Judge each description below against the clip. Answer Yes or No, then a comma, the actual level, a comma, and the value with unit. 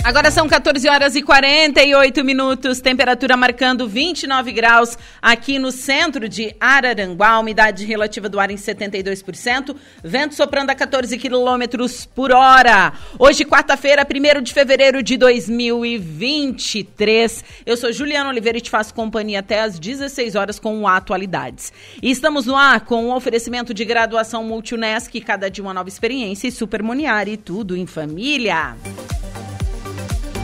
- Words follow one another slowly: No, average, 140 wpm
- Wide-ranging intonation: No, average, 4.0 semitones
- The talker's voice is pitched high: Yes, high, 235 Hz